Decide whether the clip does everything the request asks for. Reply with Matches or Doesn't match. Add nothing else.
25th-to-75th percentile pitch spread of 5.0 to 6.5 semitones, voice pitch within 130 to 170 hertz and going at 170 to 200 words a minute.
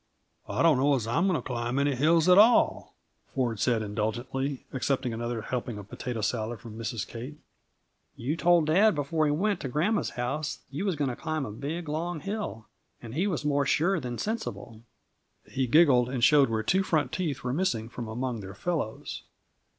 Matches